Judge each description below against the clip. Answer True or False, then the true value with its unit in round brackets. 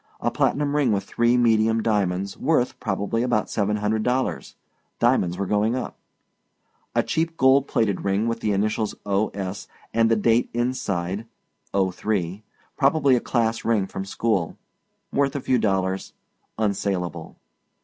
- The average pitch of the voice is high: False (110 Hz)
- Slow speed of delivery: False (145 wpm)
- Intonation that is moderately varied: True (3.5 semitones)